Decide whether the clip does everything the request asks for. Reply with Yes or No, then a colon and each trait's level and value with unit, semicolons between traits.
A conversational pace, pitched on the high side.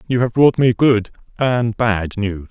No: average, 190 wpm; low, 115 Hz